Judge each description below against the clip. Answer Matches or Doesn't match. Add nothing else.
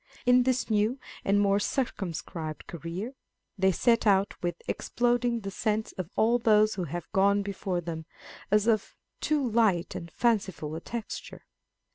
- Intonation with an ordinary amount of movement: Matches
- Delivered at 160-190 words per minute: Doesn't match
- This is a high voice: Matches